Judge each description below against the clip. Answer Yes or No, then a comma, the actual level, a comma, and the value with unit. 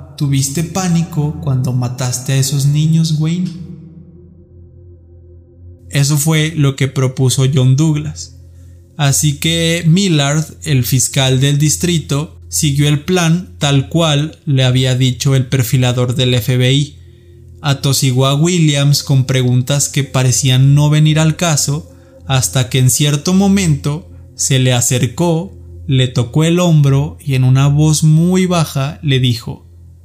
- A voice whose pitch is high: No, medium, 140 Hz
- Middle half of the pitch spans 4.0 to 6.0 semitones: No, average, 3.4 semitones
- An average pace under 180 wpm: Yes, average, 130 wpm